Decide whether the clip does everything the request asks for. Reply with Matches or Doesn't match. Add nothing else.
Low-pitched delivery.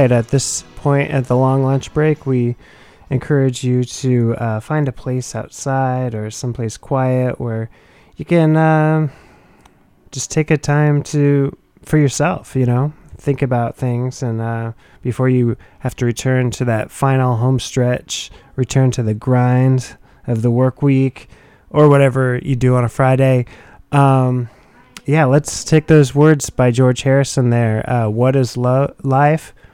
Matches